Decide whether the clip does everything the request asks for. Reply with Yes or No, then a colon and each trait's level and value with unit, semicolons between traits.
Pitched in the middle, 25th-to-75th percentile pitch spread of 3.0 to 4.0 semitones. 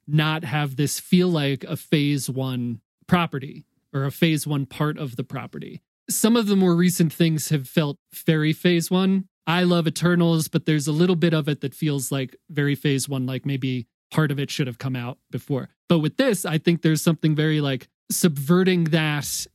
Yes: medium, 155 Hz; average, 3.7 semitones